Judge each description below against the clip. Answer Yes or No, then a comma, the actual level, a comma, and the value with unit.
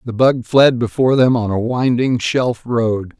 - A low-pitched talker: Yes, low, 120 Hz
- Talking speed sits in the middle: Yes, average, 190 wpm